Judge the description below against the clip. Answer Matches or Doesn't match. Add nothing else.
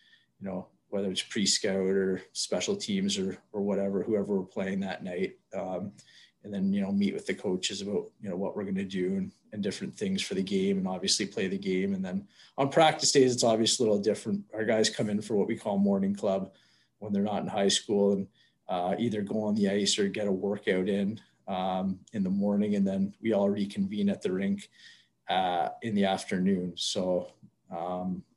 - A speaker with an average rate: Doesn't match